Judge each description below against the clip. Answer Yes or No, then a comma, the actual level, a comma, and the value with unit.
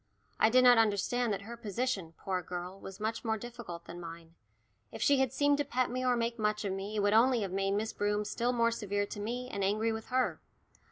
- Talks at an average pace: No, fast, 235 wpm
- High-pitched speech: Yes, high, 220 Hz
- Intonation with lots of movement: No, average, 3.6 semitones